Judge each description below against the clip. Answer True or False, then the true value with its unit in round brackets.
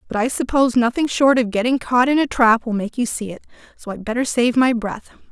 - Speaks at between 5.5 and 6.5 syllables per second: True (5.9 syllables/s)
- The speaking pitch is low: False (240 Hz)